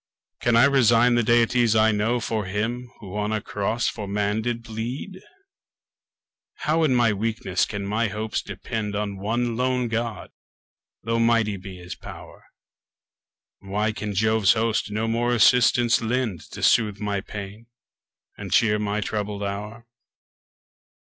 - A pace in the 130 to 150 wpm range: Yes, average, 145 wpm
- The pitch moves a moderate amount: No, narrow, 2.3 semitones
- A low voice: Yes, low, 110 Hz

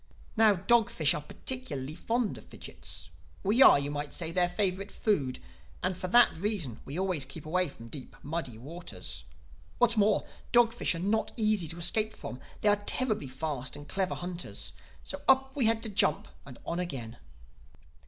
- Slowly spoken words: No, average, 175 wpm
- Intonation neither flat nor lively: No, wide, 6.8 semitones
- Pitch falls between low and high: Yes, medium, 180 Hz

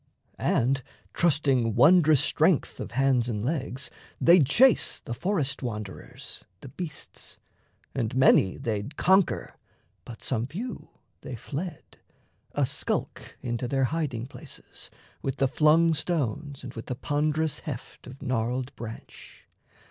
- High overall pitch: No, low, 135 Hz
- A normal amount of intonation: Yes, average, 4.4 semitones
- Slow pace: Yes, slow, 125 wpm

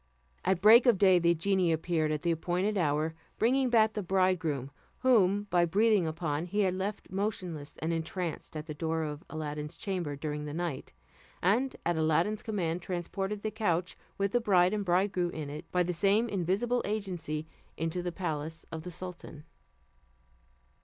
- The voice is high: No, medium, 180 Hz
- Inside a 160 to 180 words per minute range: Yes, average, 170 wpm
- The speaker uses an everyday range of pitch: Yes, average, 3.9 semitones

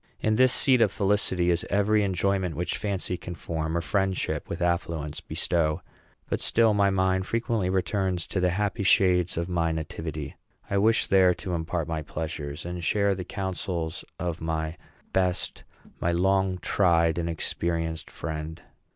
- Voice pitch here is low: Yes, very low, 90 Hz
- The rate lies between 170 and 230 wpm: No, average, 160 wpm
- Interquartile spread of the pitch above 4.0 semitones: No, average, 2.9 semitones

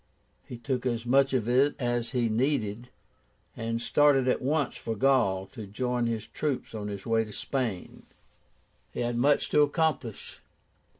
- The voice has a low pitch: Yes, low, 120 Hz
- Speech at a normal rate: Yes, average, 160 wpm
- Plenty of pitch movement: No, average, 3.1 semitones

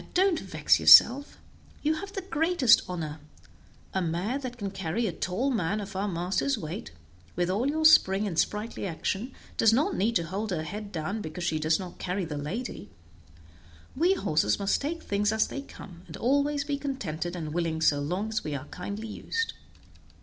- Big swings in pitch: Yes, wide, 7.7 semitones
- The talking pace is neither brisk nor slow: Yes, average, 185 wpm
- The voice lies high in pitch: Yes, high, 200 Hz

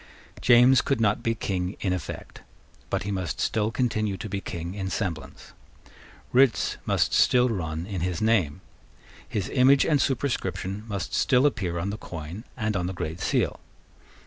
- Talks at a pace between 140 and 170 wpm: Yes, average, 165 wpm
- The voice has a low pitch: Yes, low, 100 Hz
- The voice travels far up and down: No, average, 4.3 semitones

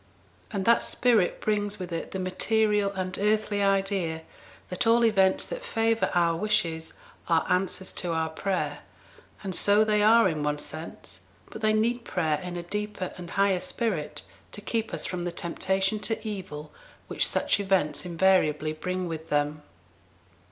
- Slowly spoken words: No, average, 160 wpm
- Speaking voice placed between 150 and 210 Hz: Yes, high, 190 Hz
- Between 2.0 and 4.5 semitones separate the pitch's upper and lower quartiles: Yes, average, 4.0 semitones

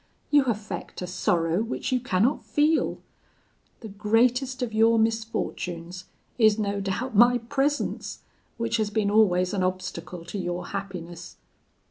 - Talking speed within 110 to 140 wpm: Yes, slow, 135 wpm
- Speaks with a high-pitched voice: Yes, high, 210 Hz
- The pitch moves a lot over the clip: No, average, 4.2 semitones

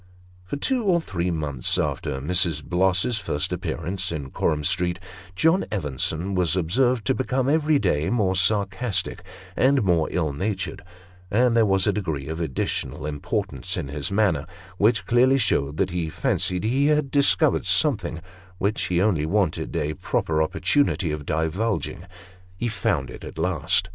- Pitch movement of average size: No, wide, 6.4 semitones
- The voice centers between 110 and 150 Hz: No, very low, 95 Hz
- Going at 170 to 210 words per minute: No, average, 155 wpm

